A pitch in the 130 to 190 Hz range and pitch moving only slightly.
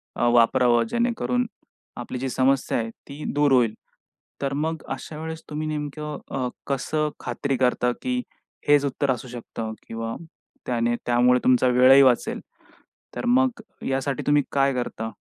No: low, 135 Hz; average, 3.4 semitones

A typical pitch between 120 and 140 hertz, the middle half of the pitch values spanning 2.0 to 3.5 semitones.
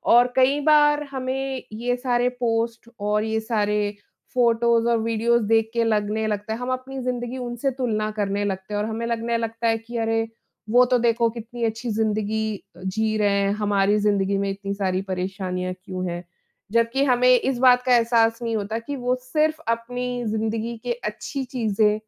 No: high, 230 Hz; average, 2.7 semitones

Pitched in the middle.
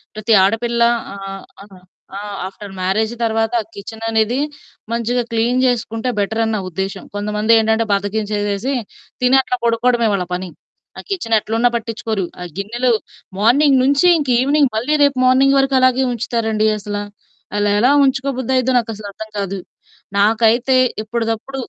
No: high, 225 Hz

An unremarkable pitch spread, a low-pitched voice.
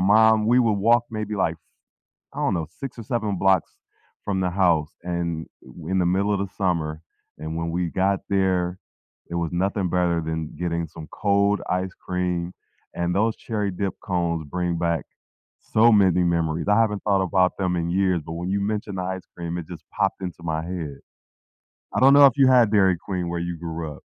Yes: average, 3.1 semitones; very low, 90 Hz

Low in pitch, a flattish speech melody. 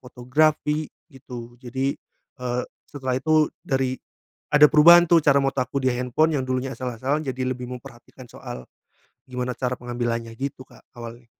Yes: low, 130 Hz; narrow, 2.1 semitones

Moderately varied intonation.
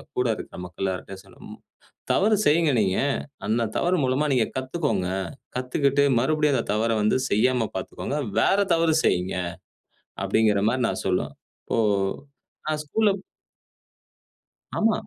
No: wide, 6.6 semitones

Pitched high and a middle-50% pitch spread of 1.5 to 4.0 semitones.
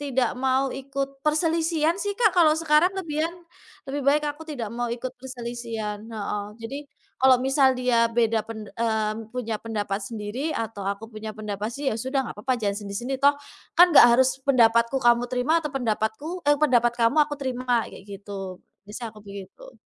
No: very high, 250 Hz; average, 4.5 semitones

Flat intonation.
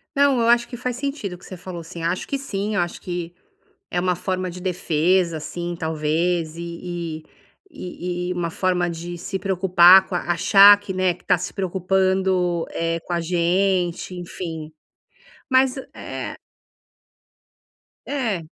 Yes: narrow, 2.0 semitones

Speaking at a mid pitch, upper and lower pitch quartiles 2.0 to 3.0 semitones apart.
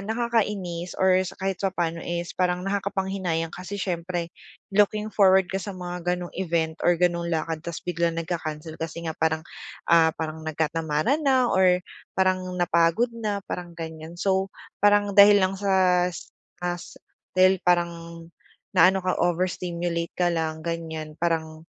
Yes: medium, 175 Hz; narrow, 2.4 semitones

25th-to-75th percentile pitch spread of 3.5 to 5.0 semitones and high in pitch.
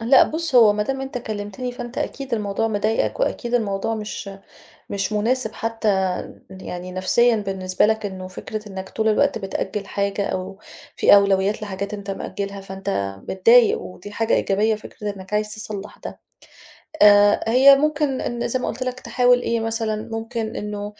No: average, 2.9 semitones; high, 215 Hz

